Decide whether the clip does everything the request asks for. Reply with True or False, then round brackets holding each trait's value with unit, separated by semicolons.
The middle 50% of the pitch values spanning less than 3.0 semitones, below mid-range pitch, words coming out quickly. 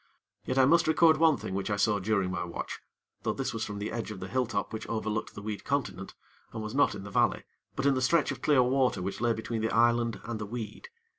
False (4.0 semitones; 115 Hz; 250 wpm)